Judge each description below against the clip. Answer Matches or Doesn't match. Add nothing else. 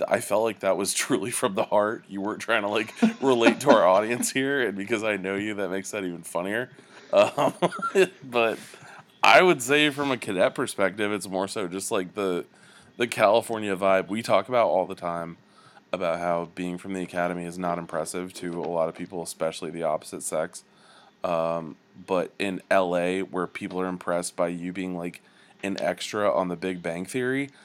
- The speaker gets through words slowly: Doesn't match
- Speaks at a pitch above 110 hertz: Doesn't match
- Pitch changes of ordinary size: Matches